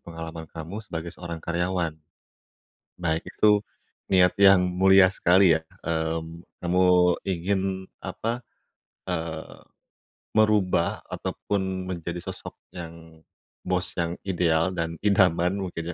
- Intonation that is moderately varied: No, narrow, 2.3 semitones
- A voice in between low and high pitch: No, very low, 90 Hz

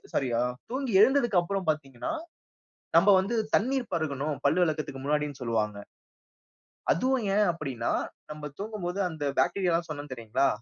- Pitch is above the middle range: No, medium, 160 Hz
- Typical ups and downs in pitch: No, wide, 6.2 semitones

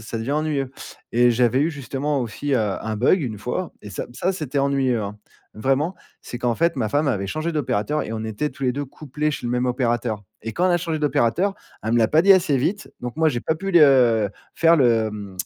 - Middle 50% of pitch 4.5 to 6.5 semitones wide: Yes, average, 5.0 semitones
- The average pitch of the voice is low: Yes, low, 130 Hz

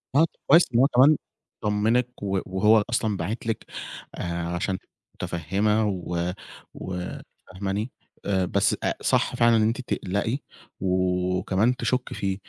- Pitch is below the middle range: Yes, low, 100 Hz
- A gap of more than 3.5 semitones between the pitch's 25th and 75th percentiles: Yes, average, 3.9 semitones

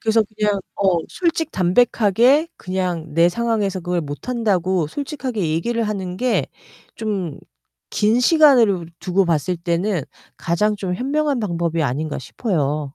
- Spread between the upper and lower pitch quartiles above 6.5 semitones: No, wide, 5.4 semitones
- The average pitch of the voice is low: No, high, 195 Hz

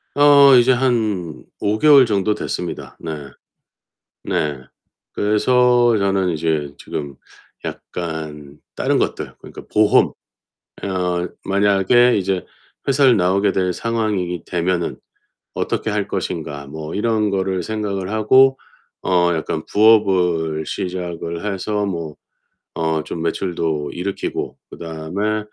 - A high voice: No, very low, 95 Hz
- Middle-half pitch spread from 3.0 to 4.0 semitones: No, average, 4.4 semitones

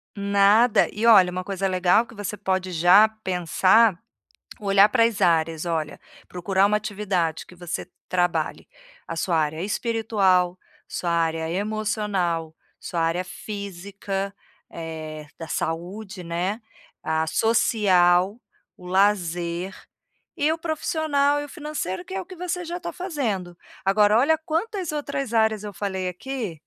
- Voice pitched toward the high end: Yes, high, 195 Hz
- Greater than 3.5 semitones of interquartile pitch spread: Yes, average, 4.1 semitones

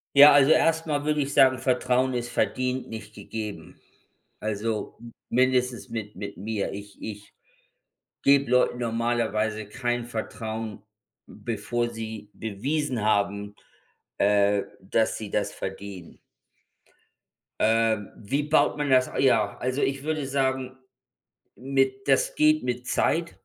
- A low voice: Yes, low, 120 Hz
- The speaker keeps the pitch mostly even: No, average, 3.7 semitones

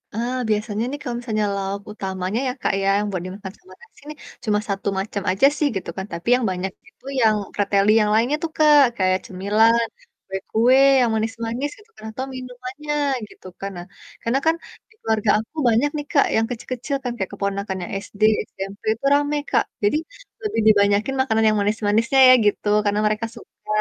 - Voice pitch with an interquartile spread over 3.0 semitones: Yes, average, 4.1 semitones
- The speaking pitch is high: Yes, high, 220 Hz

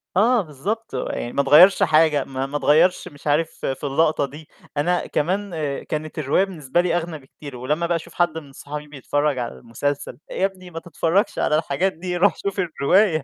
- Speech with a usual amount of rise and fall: Yes, average, 3.9 semitones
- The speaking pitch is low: No, medium, 155 Hz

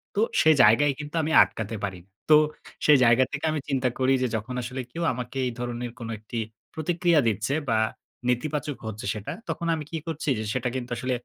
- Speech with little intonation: No, average, 4.3 semitones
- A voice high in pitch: No, low, 130 Hz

